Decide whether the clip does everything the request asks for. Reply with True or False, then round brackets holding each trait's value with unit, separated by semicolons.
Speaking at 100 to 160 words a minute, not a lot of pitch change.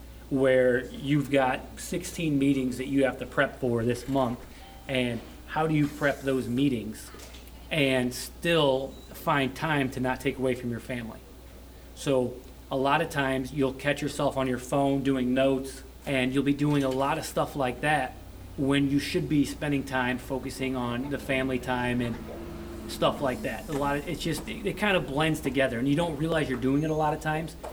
False (195 wpm; 2.1 semitones)